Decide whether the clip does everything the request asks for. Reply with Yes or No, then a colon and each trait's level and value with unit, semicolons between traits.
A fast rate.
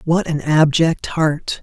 No: average, 150 wpm